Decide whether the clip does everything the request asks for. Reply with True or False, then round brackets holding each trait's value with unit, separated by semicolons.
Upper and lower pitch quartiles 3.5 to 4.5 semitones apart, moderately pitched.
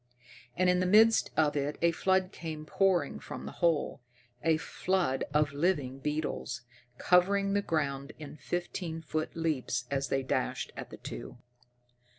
True (4.2 semitones; 160 Hz)